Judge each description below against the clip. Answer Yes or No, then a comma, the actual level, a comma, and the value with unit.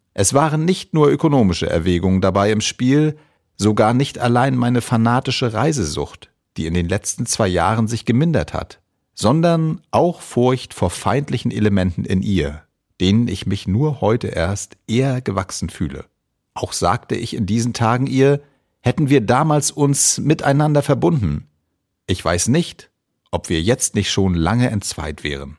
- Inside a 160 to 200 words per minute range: No, average, 150 wpm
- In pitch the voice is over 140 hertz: No, low, 115 Hz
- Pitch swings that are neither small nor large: No, wide, 6.5 semitones